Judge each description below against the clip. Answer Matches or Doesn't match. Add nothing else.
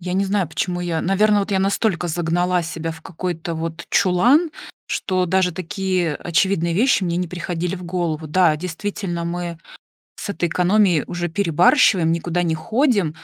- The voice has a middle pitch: Matches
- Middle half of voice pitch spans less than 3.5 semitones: Matches